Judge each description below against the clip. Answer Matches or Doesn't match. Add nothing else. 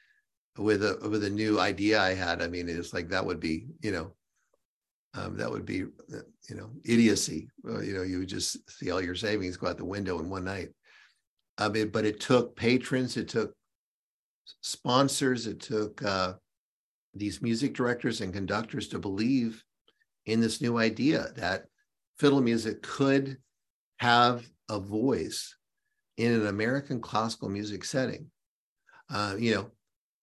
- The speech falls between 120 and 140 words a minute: Doesn't match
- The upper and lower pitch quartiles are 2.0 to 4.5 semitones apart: Matches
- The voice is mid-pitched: Doesn't match